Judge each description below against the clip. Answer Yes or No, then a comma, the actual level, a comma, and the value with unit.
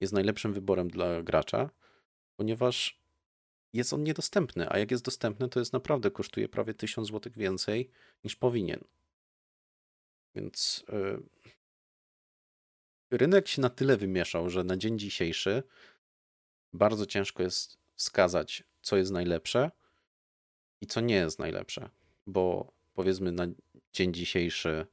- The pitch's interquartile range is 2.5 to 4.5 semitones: No, average, 4.9 semitones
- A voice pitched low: Yes, very low, 95 Hz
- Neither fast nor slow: Yes, average, 125 wpm